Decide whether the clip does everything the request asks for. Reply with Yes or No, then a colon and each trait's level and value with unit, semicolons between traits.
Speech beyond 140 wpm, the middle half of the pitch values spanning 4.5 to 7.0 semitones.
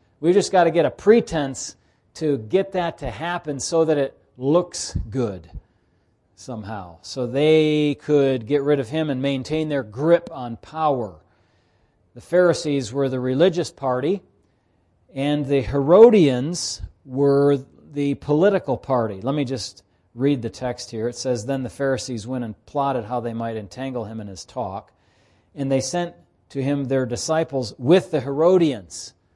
Yes: average, 155 wpm; average, 4.9 semitones